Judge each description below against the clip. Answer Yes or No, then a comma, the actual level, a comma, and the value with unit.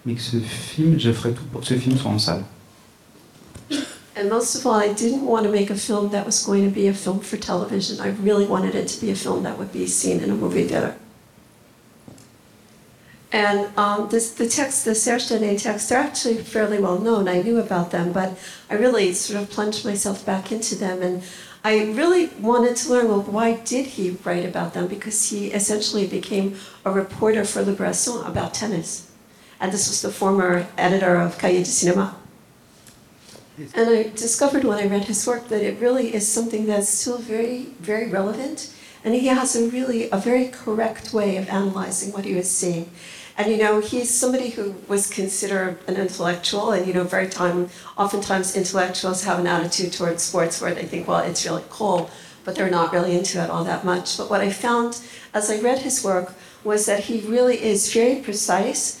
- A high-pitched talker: Yes, high, 205 Hz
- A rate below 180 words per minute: No, average, 195 wpm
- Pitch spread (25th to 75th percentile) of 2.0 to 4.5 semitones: Yes, average, 3.7 semitones